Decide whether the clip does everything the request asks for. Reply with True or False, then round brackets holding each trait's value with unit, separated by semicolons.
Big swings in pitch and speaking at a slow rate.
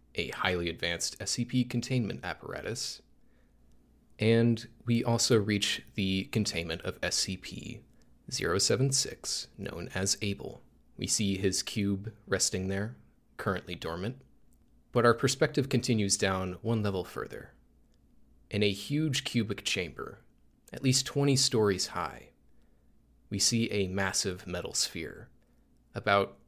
False (3.7 semitones; 115 wpm)